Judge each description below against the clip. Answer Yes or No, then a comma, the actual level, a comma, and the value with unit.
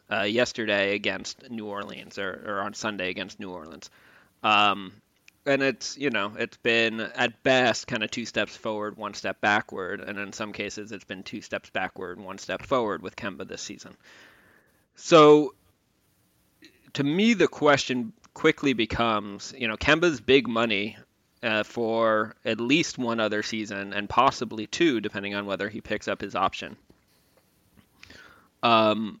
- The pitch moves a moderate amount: Yes, average, 3.3 semitones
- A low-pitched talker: Yes, low, 110 Hz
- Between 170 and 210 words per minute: No, average, 160 wpm